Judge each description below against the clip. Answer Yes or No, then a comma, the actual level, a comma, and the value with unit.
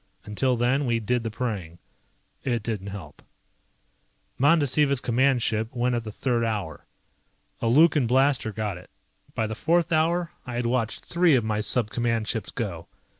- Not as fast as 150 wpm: No, average, 165 wpm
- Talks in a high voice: No, low, 120 Hz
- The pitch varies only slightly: No, average, 3.6 semitones